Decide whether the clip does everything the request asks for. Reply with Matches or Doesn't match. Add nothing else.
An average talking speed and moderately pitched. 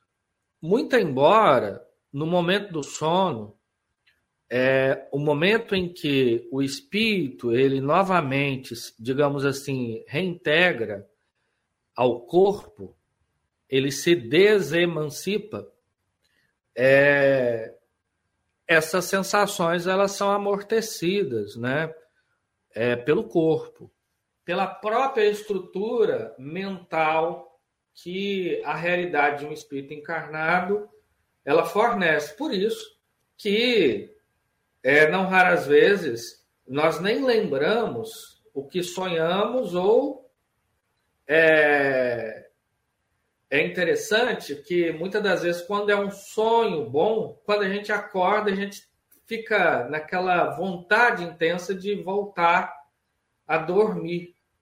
Doesn't match